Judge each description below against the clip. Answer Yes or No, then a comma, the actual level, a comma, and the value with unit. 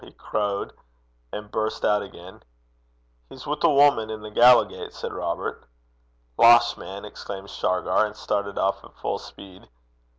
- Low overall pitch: Yes, low, 105 Hz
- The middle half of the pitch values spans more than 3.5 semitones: No, average, 2.7 semitones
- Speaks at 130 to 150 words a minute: Yes, average, 145 wpm